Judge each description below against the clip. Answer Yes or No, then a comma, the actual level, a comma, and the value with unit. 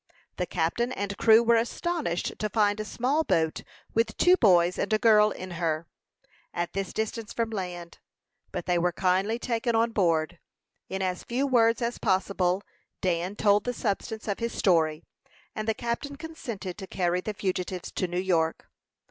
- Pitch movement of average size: Yes, average, 4.3 semitones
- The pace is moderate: Yes, average, 175 wpm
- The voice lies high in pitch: Yes, high, 200 Hz